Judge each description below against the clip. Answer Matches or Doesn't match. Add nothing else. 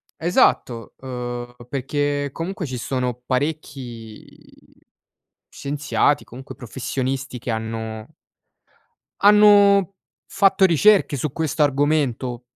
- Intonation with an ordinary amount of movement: Matches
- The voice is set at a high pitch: Doesn't match